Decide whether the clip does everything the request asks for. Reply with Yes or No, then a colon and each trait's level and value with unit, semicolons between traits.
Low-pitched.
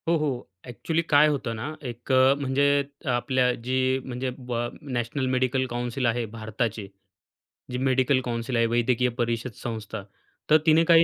Yes: low, 125 Hz